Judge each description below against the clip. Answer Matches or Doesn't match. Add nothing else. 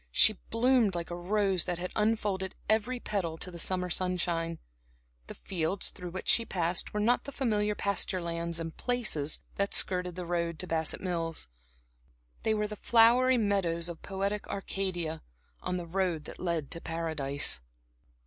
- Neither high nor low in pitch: Matches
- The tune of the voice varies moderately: Matches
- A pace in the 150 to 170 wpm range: Matches